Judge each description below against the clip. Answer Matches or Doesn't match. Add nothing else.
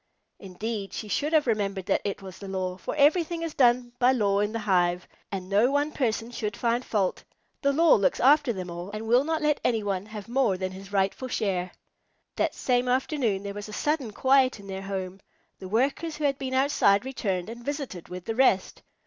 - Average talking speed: Doesn't match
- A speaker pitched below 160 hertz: Doesn't match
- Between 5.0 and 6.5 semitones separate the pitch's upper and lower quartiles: Matches